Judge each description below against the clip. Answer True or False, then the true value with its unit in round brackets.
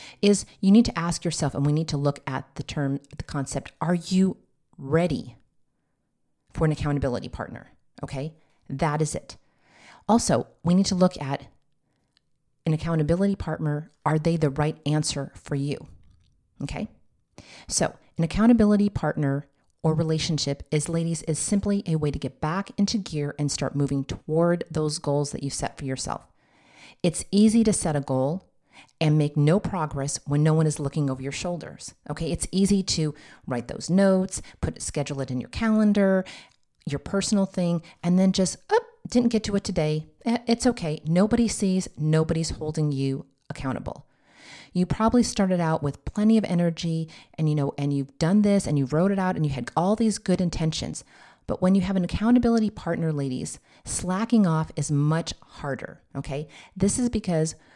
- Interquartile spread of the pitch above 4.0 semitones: True (4.8 semitones)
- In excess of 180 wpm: False (175 wpm)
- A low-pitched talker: False (160 Hz)